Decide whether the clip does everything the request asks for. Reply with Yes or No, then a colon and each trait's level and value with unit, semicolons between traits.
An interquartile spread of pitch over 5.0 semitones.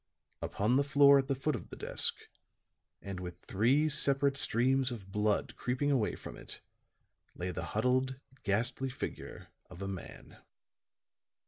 Yes: wide, 5.5 semitones